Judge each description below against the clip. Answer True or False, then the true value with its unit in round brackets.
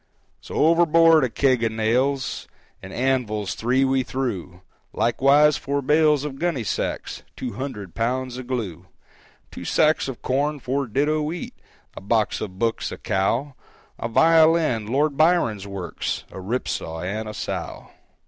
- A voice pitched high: False (130 Hz)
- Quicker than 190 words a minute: False (150 wpm)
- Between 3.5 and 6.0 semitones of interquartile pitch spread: True (5.1 semitones)